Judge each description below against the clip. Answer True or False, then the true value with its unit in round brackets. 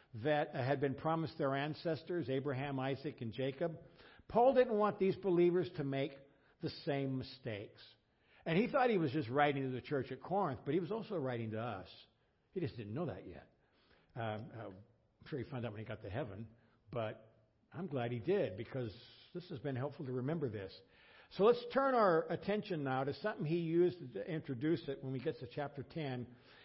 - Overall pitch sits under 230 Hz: True (140 Hz)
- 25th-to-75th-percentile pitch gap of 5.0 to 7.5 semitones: True (5.3 semitones)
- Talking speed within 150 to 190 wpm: False (200 wpm)